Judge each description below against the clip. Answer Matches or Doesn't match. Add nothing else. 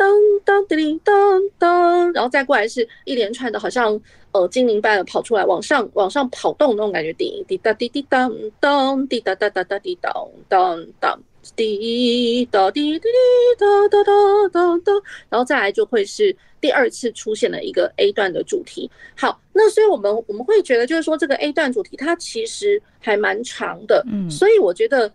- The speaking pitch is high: Matches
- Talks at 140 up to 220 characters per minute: Doesn't match